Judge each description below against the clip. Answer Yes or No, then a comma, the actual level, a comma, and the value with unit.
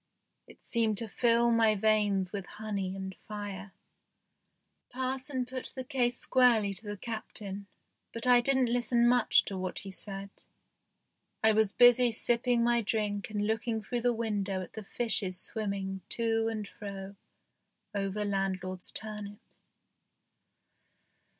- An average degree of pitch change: Yes, average, 3.1 semitones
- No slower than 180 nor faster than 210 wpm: No, slow, 135 wpm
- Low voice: No, high, 215 Hz